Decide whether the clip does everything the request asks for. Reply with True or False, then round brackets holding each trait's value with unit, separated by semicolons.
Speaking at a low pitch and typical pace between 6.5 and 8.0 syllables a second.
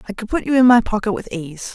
False (220 Hz; 6.6 syllables/s)